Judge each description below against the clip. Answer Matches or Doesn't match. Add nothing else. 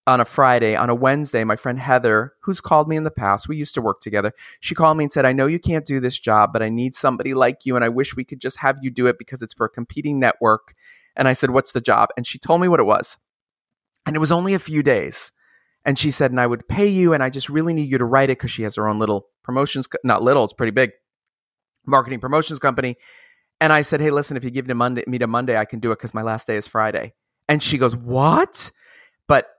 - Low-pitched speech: Matches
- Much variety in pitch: Doesn't match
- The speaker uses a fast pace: Matches